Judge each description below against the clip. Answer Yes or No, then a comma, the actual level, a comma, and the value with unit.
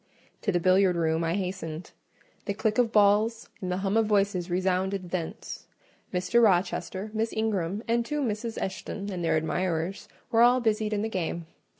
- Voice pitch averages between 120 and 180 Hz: No, high, 195 Hz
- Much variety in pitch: No, average, 3.3 semitones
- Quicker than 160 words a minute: Yes, average, 175 wpm